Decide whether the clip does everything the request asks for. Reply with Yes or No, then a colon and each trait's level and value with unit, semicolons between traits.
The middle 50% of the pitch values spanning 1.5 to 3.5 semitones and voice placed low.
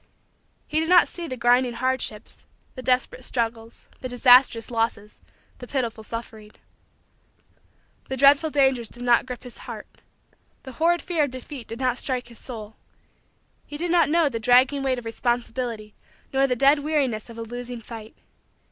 No: average, 2.9 semitones; very high, 250 Hz